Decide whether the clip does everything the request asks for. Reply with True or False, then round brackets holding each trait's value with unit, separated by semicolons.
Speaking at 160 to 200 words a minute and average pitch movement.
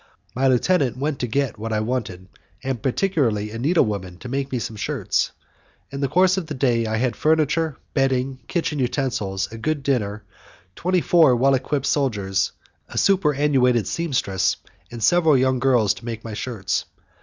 True (170 wpm; 4.6 semitones)